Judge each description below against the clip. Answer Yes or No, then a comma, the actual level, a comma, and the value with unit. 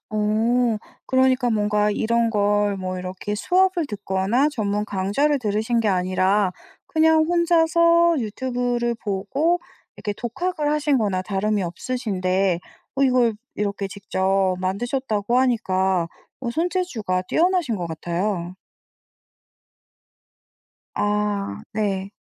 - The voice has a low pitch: No, high, 215 Hz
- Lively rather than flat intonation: No, average, 5.0 semitones